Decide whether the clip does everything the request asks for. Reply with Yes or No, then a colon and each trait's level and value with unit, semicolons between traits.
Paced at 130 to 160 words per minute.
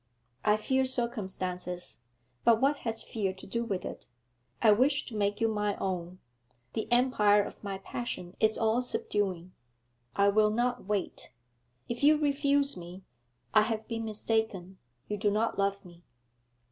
Yes: average, 155 wpm